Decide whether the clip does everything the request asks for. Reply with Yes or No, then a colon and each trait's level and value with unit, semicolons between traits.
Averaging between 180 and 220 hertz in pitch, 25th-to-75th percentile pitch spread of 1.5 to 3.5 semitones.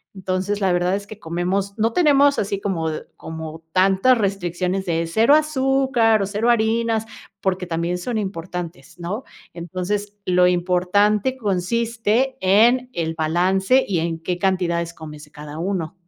No: high, 190 Hz; average, 4.1 semitones